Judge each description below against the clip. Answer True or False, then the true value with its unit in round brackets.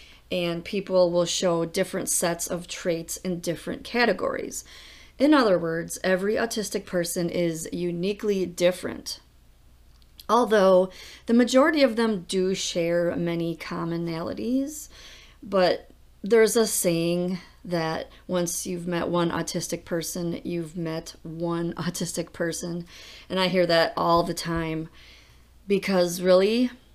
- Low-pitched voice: False (175 Hz)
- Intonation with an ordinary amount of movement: False (2.0 semitones)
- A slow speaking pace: True (120 wpm)